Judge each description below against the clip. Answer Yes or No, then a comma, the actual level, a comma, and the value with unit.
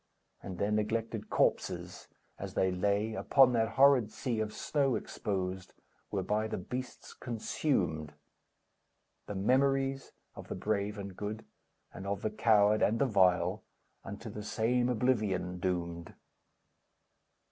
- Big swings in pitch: No, average, 3.6 semitones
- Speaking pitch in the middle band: No, low, 105 Hz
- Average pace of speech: No, slow, 130 wpm